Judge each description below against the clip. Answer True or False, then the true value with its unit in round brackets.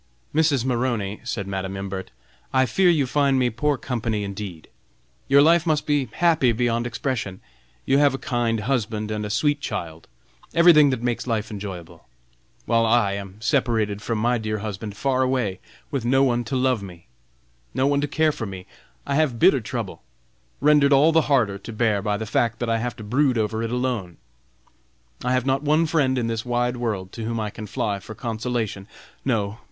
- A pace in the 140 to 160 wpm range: False (190 wpm)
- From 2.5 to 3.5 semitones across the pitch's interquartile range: False (4.2 semitones)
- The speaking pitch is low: True (120 Hz)